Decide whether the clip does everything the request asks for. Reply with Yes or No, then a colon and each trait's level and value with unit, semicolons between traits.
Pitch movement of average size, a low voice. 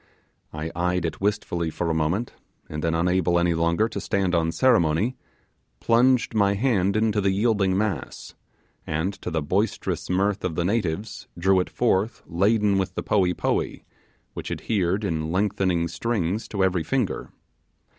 Yes: average, 3.7 semitones; very low, 95 Hz